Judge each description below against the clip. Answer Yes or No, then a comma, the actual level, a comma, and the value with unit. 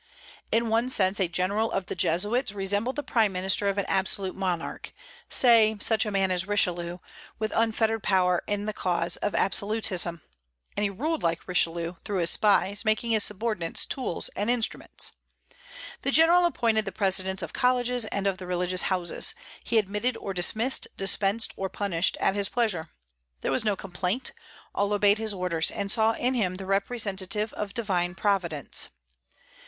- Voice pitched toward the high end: Yes, high, 200 Hz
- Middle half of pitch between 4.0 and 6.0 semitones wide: No, average, 3.2 semitones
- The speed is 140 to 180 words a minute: Yes, average, 170 wpm